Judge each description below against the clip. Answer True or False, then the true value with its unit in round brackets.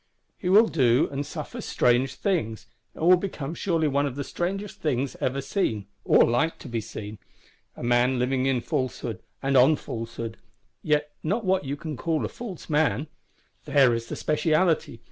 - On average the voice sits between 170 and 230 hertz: False (140 Hz)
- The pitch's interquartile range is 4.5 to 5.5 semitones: True (5.0 semitones)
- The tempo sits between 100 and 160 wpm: False (175 wpm)